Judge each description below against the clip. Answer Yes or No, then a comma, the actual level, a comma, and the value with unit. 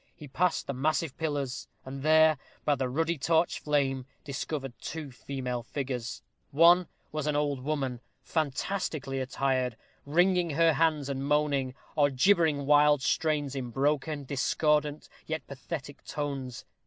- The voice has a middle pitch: Yes, medium, 145 Hz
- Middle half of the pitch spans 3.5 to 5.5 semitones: No, average, 2.7 semitones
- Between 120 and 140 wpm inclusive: Yes, slow, 135 wpm